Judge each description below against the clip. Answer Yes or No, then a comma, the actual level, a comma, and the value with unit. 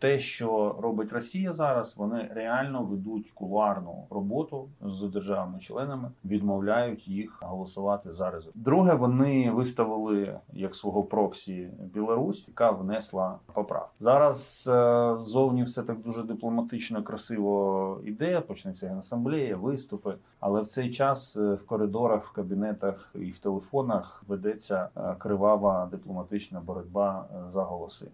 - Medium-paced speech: Yes, average, 120 wpm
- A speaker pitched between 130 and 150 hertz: No, low, 110 Hz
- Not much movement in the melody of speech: No, average, 3.7 semitones